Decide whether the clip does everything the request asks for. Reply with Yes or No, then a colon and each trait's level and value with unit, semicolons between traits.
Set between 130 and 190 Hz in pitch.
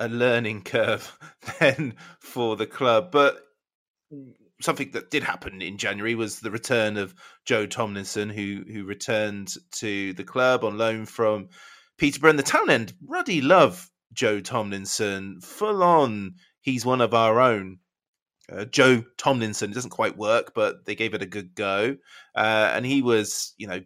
No: low, 110 Hz